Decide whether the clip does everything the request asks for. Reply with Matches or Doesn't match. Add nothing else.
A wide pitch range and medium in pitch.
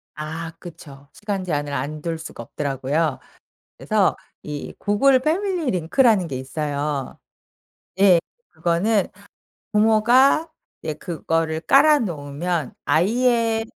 Matches